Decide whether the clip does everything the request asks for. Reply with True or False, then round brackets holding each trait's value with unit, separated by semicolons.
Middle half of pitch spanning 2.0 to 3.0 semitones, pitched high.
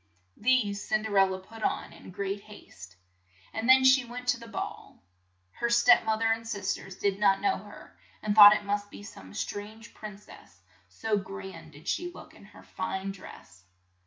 True (2.6 semitones; 205 Hz)